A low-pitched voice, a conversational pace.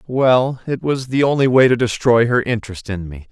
No: low, 120 Hz; fast, 215 wpm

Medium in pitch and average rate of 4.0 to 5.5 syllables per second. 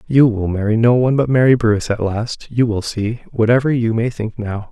No: low, 115 Hz; 5.4 syllables/s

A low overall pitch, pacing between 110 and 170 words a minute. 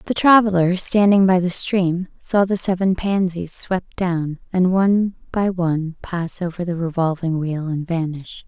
No: medium, 180 Hz; average, 165 wpm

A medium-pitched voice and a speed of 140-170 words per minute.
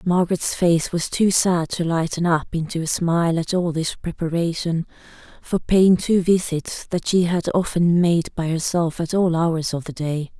No: medium, 170 Hz; average, 185 wpm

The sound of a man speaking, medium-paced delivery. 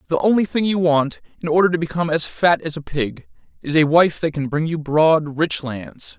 No: male; fast, 235 wpm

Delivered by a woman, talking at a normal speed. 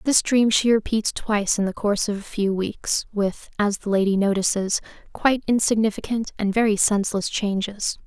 Yes: female; average, 155 wpm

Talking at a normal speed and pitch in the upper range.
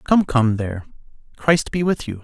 No: average, 190 wpm; low, 130 Hz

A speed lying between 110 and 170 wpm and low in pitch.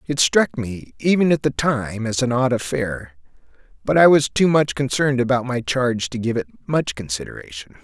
No: average, 190 wpm; low, 125 Hz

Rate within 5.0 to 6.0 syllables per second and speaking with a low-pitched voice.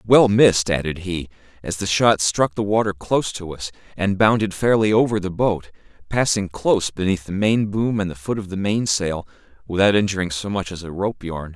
Yes: 5.3 syllables/s; very low, 95 Hz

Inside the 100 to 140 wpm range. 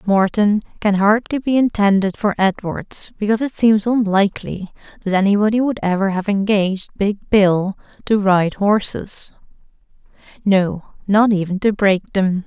Yes: slow, 135 wpm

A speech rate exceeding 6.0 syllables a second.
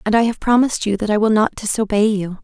Yes: 6.5 syllables/s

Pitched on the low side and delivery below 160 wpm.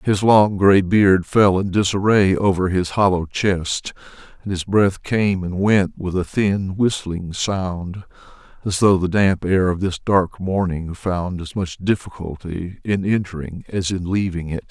No: very low, 95 Hz; average, 165 wpm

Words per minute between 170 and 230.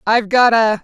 Yes: fast, 215 wpm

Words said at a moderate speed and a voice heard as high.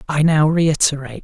No: average, 145 wpm; medium, 150 Hz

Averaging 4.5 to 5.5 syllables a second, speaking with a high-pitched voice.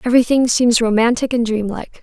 No: 6.2 syllables/s; high, 235 Hz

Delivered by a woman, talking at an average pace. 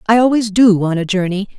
No: female; fast, 225 wpm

